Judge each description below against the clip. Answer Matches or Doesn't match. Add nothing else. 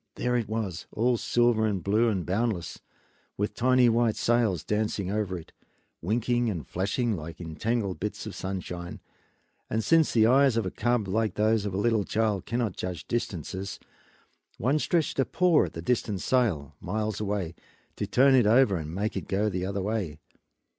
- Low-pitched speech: Matches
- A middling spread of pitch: Matches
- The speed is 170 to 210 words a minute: Matches